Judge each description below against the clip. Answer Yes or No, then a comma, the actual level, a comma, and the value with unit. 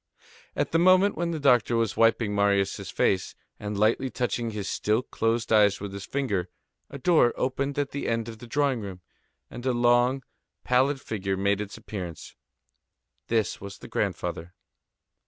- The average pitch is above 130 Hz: No, low, 115 Hz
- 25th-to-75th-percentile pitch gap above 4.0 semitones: Yes, average, 4.4 semitones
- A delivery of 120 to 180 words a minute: Yes, average, 165 wpm